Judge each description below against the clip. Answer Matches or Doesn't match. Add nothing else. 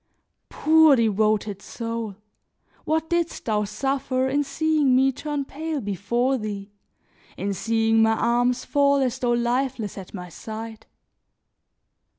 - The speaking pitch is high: Matches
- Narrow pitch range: Doesn't match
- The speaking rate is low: Matches